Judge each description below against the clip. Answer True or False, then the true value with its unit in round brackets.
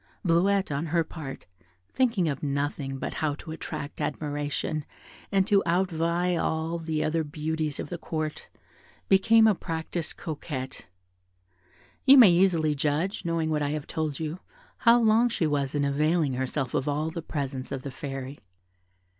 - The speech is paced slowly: False (155 wpm)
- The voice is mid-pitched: True (155 Hz)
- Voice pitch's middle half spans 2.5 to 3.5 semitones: True (3.0 semitones)